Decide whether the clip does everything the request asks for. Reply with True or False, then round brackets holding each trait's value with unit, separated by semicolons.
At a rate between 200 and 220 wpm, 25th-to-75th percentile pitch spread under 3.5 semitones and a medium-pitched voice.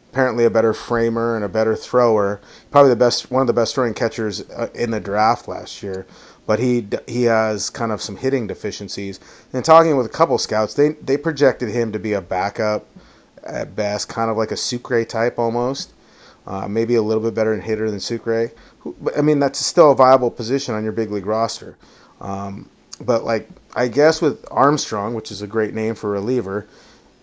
False (205 wpm; 2.6 semitones; 115 Hz)